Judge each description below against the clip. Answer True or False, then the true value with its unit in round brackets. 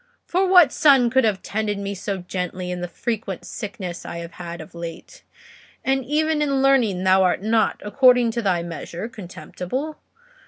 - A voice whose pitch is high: True (210 Hz)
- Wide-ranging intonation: True (6.6 semitones)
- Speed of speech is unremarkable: True (170 wpm)